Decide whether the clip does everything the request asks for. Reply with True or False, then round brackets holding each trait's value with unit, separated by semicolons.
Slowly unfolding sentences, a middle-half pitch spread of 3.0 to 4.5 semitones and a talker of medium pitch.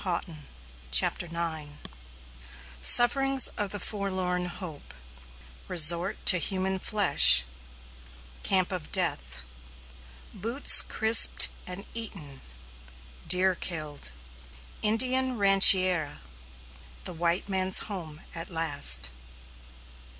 True (85 wpm; 4.1 semitones; 180 Hz)